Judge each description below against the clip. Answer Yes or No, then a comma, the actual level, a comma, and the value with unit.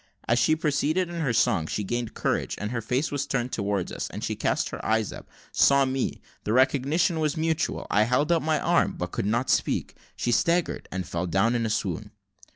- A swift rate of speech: Yes, fast, 215 wpm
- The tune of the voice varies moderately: No, wide, 6.2 semitones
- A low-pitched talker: Yes, low, 125 Hz